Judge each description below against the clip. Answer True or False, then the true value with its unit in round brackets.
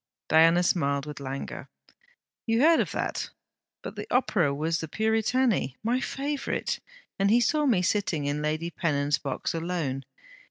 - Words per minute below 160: True (150 wpm)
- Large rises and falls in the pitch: True (7.3 semitones)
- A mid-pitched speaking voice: True (170 Hz)